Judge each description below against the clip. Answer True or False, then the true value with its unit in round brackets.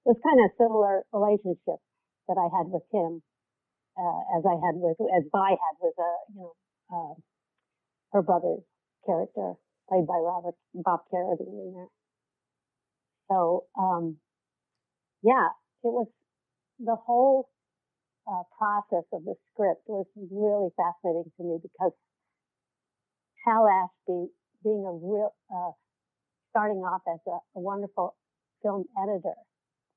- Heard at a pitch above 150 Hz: True (190 Hz)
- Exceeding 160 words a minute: False (135 wpm)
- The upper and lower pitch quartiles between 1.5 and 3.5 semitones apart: True (3.2 semitones)